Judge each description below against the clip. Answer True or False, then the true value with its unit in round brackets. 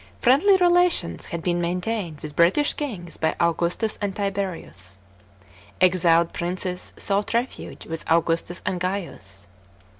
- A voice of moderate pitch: True (180 Hz)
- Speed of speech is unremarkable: False (120 wpm)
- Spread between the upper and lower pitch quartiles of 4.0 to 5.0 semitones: False (3.5 semitones)